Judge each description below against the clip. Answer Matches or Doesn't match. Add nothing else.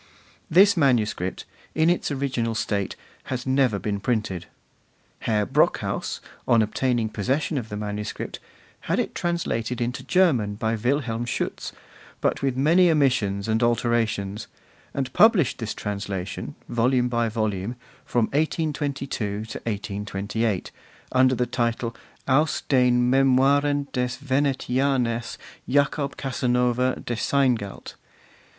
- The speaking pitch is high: Doesn't match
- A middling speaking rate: Doesn't match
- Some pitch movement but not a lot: Matches